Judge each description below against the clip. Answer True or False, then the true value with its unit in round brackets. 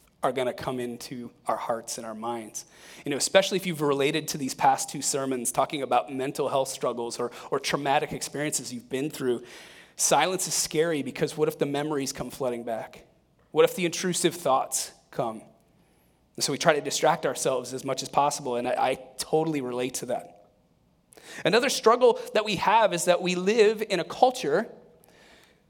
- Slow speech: False (185 wpm)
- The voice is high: False (140 Hz)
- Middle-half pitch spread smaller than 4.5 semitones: False (5.5 semitones)